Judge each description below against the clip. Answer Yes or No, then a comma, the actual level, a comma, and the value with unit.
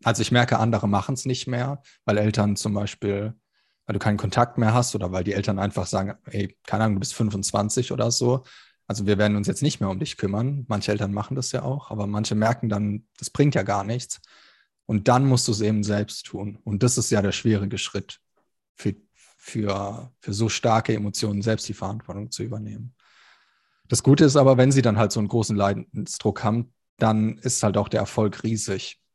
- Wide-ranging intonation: No, average, 2.9 semitones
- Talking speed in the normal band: No, fast, 210 wpm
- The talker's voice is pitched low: Yes, low, 110 Hz